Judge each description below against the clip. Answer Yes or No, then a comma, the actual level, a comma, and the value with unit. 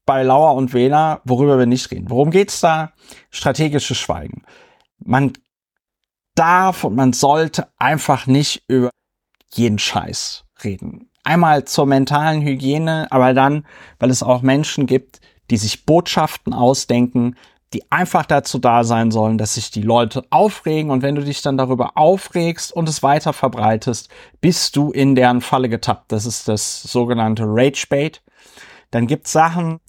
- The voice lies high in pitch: No, low, 135 Hz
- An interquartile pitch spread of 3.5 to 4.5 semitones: Yes, average, 4.1 semitones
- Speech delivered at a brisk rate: No, average, 155 wpm